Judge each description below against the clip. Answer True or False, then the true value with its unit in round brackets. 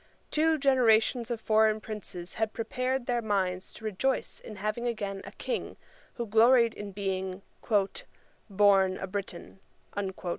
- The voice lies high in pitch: True (215 Hz)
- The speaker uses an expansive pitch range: False (3.4 semitones)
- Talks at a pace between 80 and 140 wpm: True (135 wpm)